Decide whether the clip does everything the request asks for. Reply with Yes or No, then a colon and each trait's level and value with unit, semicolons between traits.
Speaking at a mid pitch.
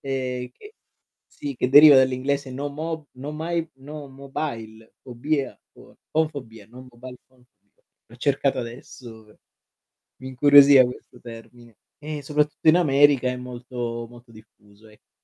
No: low, 130 Hz